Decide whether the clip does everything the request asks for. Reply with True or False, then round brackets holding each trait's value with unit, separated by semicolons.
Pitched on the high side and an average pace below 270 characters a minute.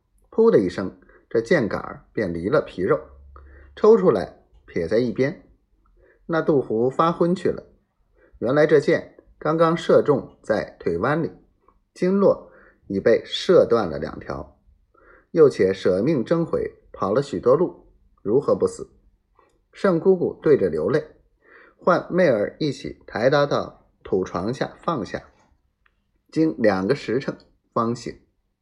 True (225 Hz; 185 characters per minute)